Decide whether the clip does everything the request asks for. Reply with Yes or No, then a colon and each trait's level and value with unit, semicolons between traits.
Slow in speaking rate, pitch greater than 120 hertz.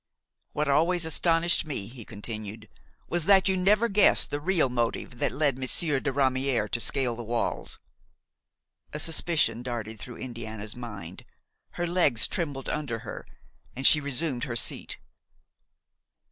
No: average, 145 wpm; low, 135 Hz